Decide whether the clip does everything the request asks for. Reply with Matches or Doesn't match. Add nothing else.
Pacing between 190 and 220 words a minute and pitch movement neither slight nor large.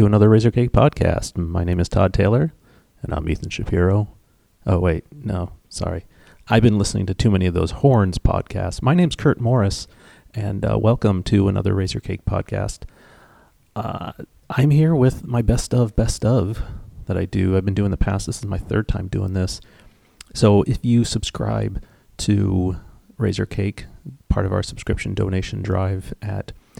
Doesn't match